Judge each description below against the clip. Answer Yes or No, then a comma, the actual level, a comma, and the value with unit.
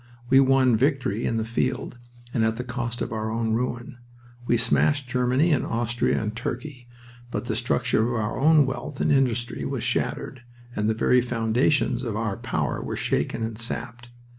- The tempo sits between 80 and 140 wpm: No, average, 180 wpm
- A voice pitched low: Yes, low, 120 Hz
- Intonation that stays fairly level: Yes, narrow, 2.3 semitones